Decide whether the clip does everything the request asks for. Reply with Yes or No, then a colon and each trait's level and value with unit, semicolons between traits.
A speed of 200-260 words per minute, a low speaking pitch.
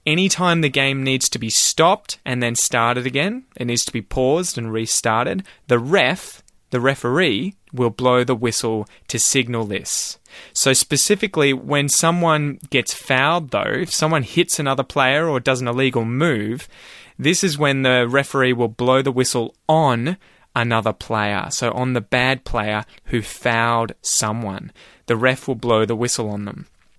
No: average, 165 wpm; low, 125 Hz